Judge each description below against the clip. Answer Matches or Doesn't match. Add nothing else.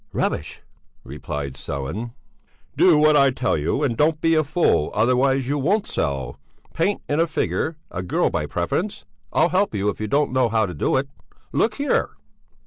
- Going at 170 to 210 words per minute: Matches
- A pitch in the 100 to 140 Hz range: Matches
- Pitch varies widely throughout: Matches